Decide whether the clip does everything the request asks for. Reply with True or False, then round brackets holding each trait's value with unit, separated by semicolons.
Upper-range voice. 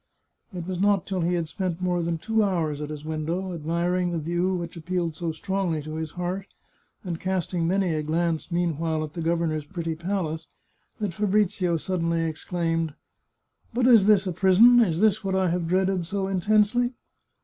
False (175 Hz)